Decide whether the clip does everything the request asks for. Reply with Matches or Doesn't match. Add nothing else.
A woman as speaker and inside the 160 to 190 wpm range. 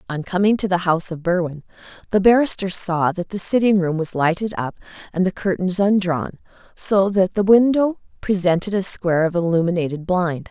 Matches